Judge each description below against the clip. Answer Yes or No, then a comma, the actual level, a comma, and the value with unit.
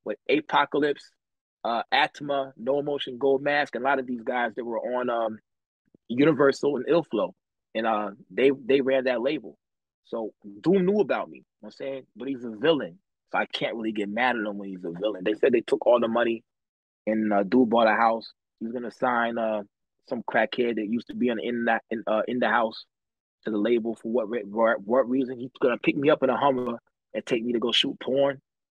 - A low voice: Yes, low, 120 Hz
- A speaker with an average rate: No, fast, 230 wpm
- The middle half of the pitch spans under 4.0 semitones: Yes, average, 3.5 semitones